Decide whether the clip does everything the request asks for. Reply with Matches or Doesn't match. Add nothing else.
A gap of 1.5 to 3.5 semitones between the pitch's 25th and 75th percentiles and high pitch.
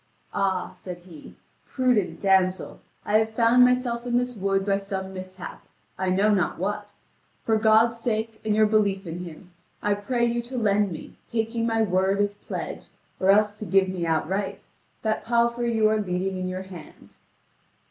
Matches